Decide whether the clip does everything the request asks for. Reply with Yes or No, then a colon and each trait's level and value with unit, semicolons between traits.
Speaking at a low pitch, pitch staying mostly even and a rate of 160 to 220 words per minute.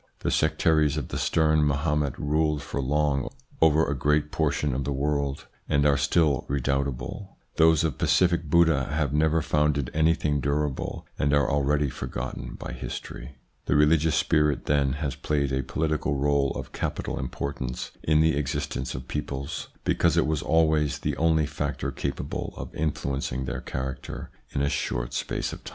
Yes: very low, 75 Hz; narrow, 2.0 semitones; average, 165 wpm